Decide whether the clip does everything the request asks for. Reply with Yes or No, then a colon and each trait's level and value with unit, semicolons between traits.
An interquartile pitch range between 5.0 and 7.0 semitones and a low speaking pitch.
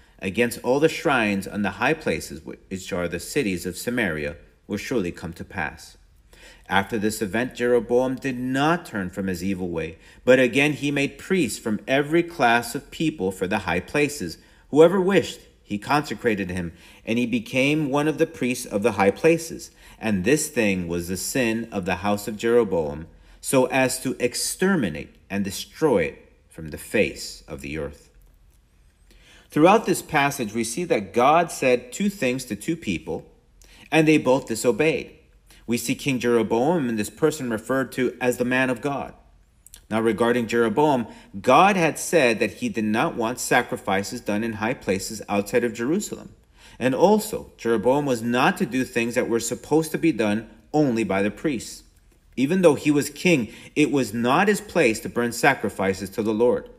Yes: wide, 5.6 semitones; low, 120 Hz